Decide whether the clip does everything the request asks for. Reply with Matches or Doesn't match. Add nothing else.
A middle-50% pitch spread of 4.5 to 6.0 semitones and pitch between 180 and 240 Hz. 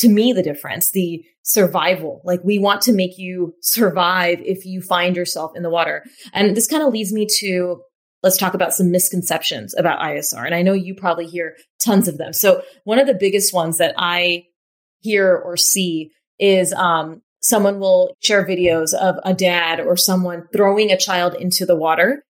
Doesn't match